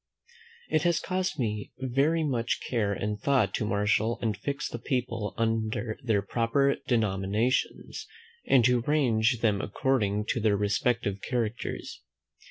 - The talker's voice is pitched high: No, low, 115 Hz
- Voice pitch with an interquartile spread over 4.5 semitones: No, average, 3.9 semitones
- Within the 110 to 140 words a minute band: Yes, slow, 135 wpm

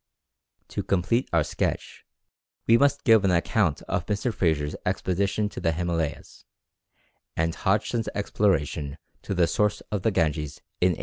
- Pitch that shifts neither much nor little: Yes, average, 4.3 semitones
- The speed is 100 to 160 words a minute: Yes, average, 145 wpm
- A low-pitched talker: Yes, very low, 90 Hz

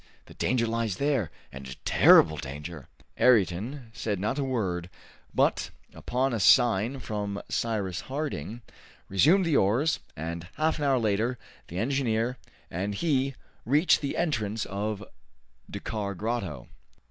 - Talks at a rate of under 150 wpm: Yes, slow, 135 wpm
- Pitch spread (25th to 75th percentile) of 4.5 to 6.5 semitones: Yes, wide, 5.5 semitones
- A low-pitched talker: Yes, low, 110 Hz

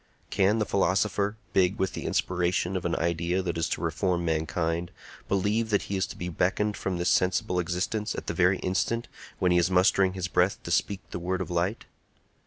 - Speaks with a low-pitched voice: Yes, very low, 90 Hz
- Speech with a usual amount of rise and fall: No, narrow, 1.9 semitones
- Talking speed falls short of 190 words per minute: No, average, 200 wpm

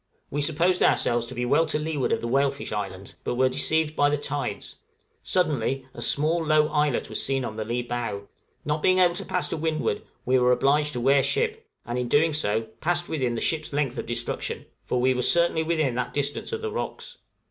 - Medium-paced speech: No, fast, 215 wpm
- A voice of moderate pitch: Yes, medium, 145 Hz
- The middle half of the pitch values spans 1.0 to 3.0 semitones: No, average, 4.4 semitones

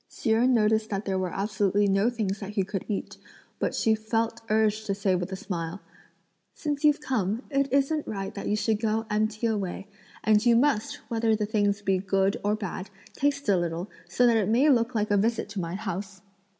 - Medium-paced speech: No, fast, 210 wpm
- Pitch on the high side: Yes, high, 215 Hz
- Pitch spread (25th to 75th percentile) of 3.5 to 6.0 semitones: No, average, 2.7 semitones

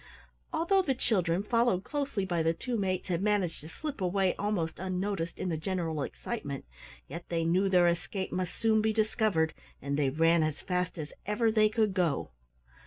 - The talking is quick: No, average, 180 wpm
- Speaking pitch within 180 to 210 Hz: Yes, medium, 185 Hz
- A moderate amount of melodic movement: Yes, average, 4.4 semitones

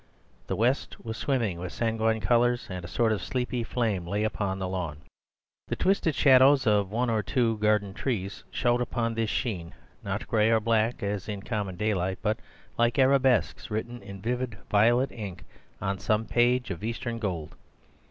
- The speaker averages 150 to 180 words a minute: Yes, average, 175 wpm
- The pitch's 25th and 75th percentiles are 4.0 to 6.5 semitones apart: No, average, 3.3 semitones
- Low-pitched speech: Yes, low, 110 Hz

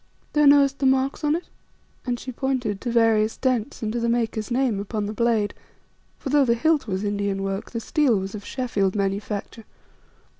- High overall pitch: Yes, high, 230 Hz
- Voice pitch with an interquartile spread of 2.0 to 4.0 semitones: No, average, 4.4 semitones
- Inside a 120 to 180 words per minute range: No, average, 190 wpm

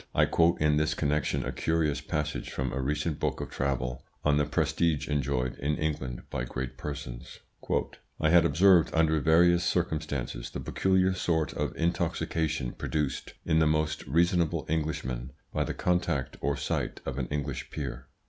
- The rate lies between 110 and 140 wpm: No, average, 160 wpm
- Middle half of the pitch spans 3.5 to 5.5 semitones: No, average, 3.1 semitones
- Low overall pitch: Yes, very low, 75 Hz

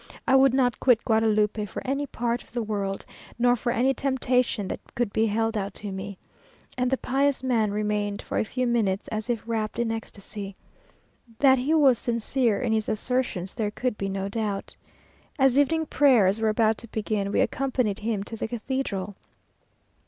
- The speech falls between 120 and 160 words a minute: No, average, 185 wpm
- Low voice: No, high, 225 Hz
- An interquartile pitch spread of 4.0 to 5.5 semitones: No, average, 3.3 semitones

